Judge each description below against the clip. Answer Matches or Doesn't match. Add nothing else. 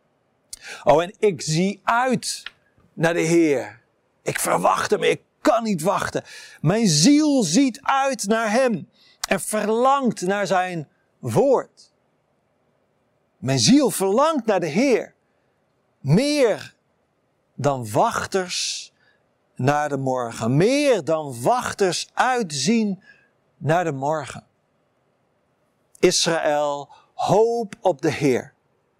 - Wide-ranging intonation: Matches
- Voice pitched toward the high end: Matches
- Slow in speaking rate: Matches